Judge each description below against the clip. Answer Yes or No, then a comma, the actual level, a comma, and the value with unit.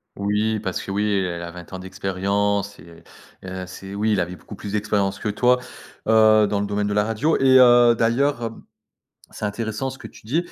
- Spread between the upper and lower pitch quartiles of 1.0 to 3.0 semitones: Yes, narrow, 2.6 semitones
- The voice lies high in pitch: No, low, 105 Hz